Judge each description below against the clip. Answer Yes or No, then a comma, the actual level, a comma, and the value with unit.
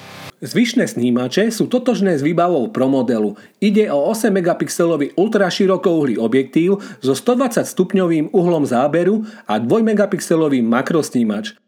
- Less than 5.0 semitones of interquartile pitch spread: No, wide, 6.4 semitones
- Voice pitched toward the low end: No, medium, 185 Hz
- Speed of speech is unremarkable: Yes, average, 120 wpm